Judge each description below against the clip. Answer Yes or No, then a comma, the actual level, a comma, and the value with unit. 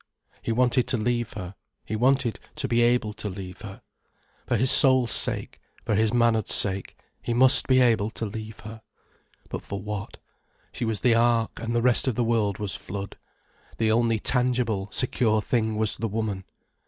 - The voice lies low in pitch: Yes, low, 115 Hz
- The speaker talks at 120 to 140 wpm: No, average, 180 wpm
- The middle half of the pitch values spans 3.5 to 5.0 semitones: No, narrow, 2.4 semitones